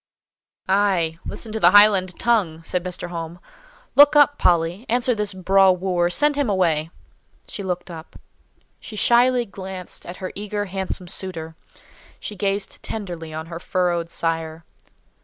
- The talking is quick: No, average, 145 wpm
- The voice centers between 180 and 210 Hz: Yes, medium, 185 Hz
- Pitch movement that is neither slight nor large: Yes, average, 3.3 semitones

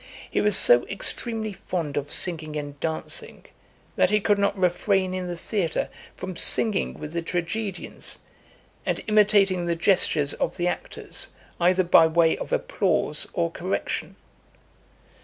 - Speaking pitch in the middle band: Yes, medium, 180 Hz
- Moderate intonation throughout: Yes, average, 3.6 semitones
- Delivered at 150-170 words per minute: No, average, 140 wpm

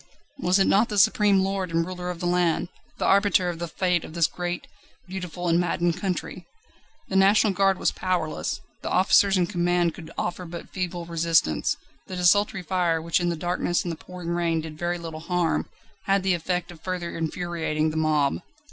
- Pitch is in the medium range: Yes, medium, 175 Hz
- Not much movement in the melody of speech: Yes, narrow, 1.8 semitones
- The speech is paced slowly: No, average, 190 wpm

